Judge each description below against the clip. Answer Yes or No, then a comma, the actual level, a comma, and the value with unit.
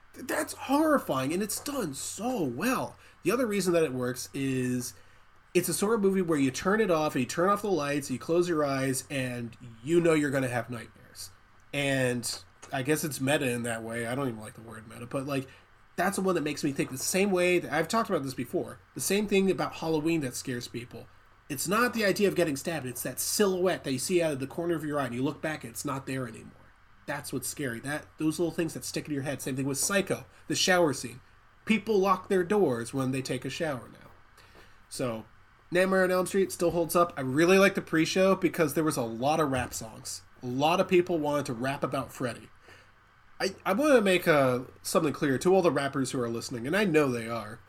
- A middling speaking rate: No, fast, 240 wpm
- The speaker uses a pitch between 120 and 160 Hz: Yes, medium, 140 Hz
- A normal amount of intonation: No, wide, 5.8 semitones